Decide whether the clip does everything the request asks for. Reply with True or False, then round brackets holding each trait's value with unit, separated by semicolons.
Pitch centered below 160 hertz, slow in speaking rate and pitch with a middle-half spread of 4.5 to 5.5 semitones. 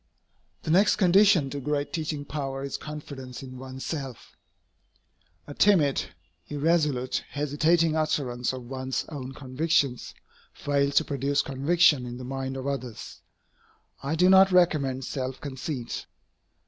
False (140 Hz; 130 wpm; 3.0 semitones)